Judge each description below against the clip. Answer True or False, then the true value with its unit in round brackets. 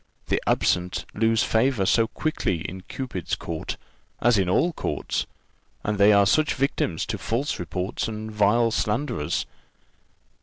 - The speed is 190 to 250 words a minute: False (145 wpm)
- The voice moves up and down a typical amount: True (4.3 semitones)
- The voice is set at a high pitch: False (105 Hz)